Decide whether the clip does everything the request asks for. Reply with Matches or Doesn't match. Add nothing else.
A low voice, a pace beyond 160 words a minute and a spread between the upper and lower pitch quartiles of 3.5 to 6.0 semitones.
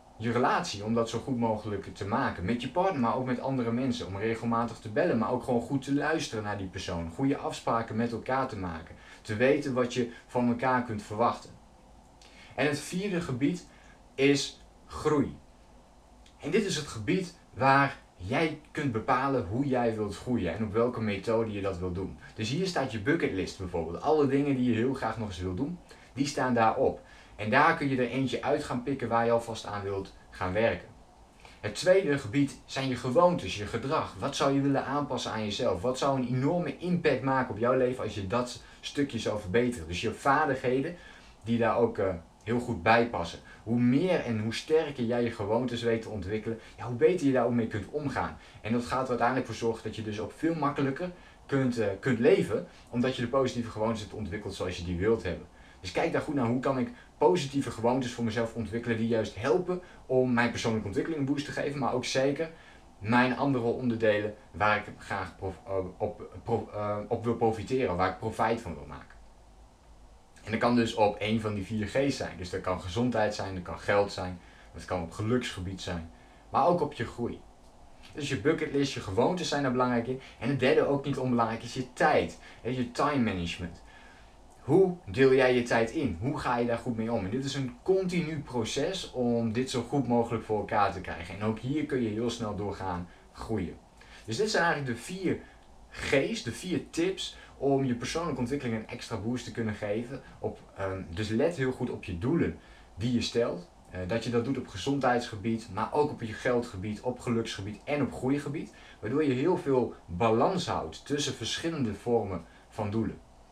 Matches